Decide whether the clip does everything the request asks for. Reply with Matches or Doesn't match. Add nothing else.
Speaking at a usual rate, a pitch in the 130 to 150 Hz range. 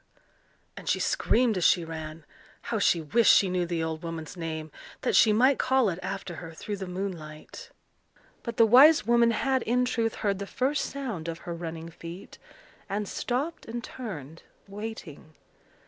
Doesn't match